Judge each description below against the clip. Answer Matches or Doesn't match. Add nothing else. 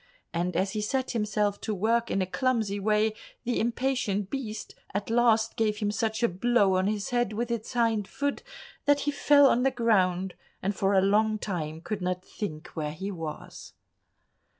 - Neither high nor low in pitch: Doesn't match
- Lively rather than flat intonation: Doesn't match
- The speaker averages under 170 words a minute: Doesn't match